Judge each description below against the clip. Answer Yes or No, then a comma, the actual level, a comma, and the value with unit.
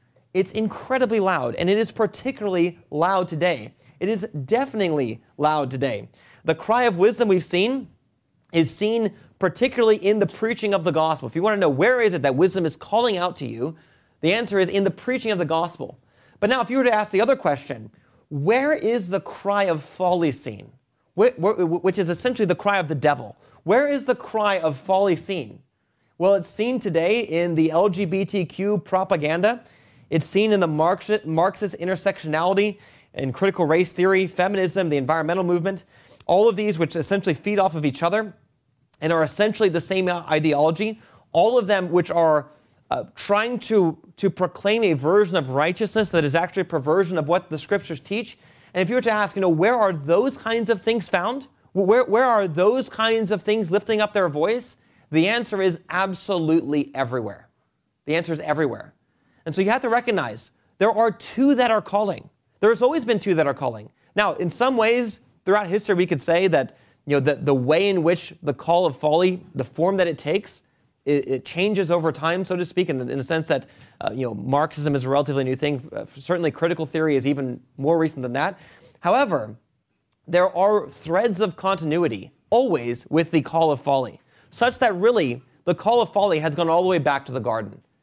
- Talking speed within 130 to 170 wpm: No, average, 200 wpm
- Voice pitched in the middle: Yes, medium, 180 Hz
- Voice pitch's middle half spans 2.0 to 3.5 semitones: No, average, 5.2 semitones